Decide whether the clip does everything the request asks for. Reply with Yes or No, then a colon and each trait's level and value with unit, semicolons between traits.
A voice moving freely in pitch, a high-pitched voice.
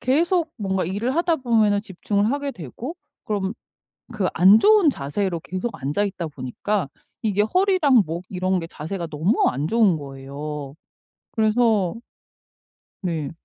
Yes: wide, 6.2 semitones; high, 200 Hz